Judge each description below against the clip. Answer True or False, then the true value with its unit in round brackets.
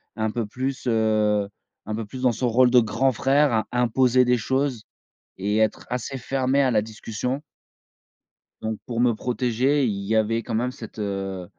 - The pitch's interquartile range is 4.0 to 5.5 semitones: False (2.9 semitones)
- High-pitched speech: False (115 Hz)